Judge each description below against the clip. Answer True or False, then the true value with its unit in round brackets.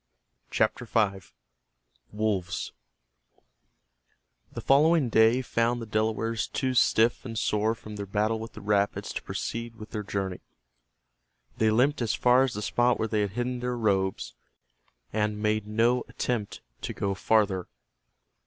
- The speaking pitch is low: True (110 Hz)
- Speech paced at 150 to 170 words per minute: False (140 wpm)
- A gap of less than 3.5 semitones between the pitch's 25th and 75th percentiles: True (2.6 semitones)